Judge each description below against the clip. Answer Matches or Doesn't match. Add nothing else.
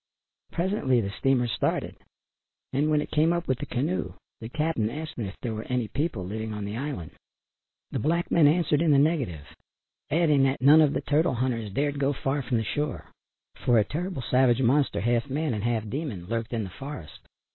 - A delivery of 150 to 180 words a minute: Doesn't match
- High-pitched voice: Doesn't match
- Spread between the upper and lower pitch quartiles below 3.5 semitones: Doesn't match